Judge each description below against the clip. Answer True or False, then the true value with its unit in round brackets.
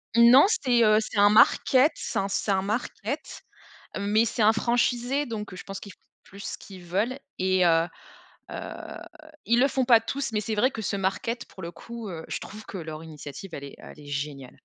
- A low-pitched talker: False (210 Hz)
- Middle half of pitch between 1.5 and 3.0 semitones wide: False (4.2 semitones)